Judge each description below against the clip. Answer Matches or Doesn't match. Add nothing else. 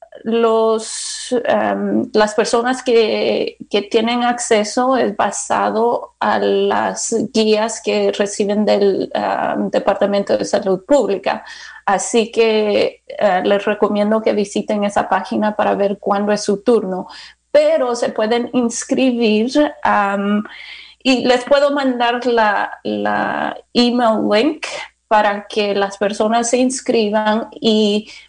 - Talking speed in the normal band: Doesn't match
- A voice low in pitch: Doesn't match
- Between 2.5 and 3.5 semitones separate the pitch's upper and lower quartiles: Matches